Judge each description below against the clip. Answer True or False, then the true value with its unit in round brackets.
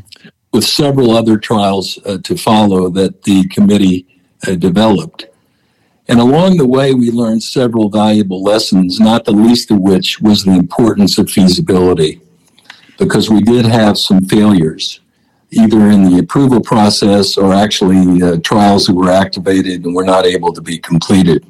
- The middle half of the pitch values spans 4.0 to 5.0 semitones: False (3.2 semitones)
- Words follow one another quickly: False (155 wpm)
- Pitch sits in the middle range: False (105 Hz)